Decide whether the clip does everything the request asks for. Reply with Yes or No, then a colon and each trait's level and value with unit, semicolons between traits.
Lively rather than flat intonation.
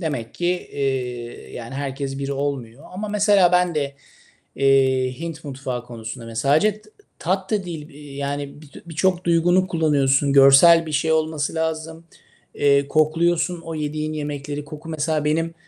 No: average, 3.2 semitones